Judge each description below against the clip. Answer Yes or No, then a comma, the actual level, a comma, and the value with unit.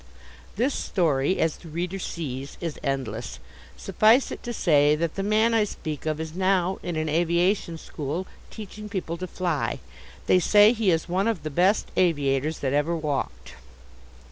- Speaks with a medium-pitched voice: Yes, medium, 170 Hz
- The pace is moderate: Yes, average, 170 wpm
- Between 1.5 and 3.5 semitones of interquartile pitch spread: No, average, 4.1 semitones